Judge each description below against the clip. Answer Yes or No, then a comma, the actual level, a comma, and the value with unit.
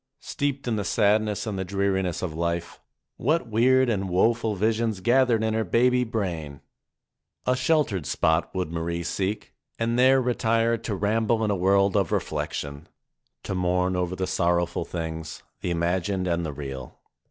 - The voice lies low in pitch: Yes, low, 100 Hz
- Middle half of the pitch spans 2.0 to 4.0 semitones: No, average, 4.7 semitones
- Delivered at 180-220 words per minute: No, average, 165 wpm